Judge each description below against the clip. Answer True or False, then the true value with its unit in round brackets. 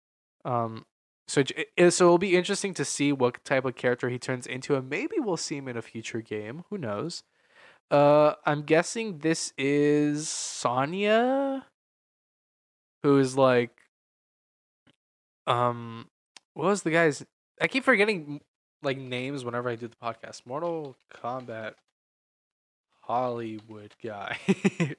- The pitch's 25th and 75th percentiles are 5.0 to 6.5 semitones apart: True (5.4 semitones)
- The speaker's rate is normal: False (130 wpm)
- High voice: False (140 Hz)